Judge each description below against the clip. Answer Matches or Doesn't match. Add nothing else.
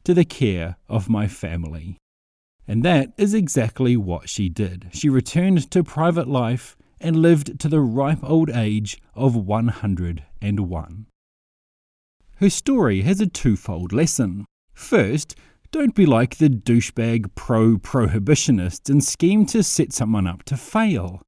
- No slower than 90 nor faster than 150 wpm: Matches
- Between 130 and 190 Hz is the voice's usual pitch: Doesn't match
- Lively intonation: Matches